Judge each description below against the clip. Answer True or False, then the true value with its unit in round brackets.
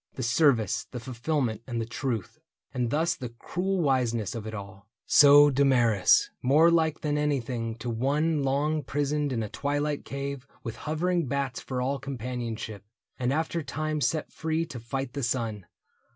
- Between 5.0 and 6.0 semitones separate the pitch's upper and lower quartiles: False (4.1 semitones)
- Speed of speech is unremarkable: True (165 wpm)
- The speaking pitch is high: False (135 Hz)